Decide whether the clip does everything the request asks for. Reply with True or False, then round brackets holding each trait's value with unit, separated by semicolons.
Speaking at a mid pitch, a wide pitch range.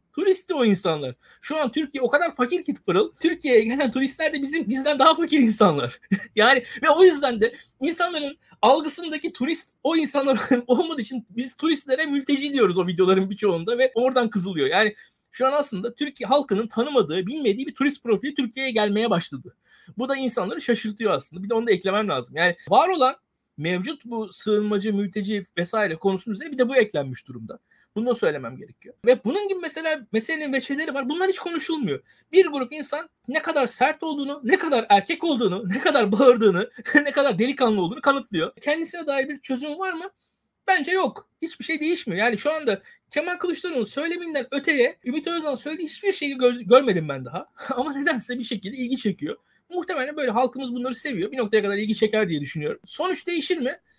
False (260 Hz; 6.2 semitones)